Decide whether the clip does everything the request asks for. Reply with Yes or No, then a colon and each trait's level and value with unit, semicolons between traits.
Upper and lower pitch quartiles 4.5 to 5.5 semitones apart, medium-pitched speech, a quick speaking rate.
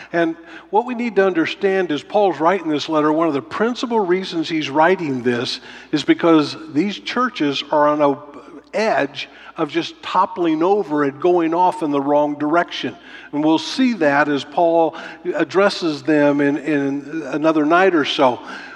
No: average, 5.2 semitones; medium, 165 Hz; average, 165 wpm